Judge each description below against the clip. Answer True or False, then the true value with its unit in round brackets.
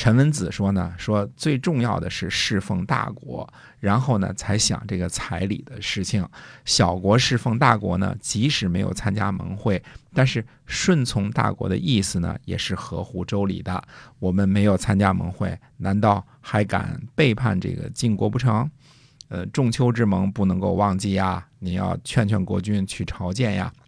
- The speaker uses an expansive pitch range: False (4.5 semitones)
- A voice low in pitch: True (105 Hz)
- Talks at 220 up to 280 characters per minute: True (250 characters per minute)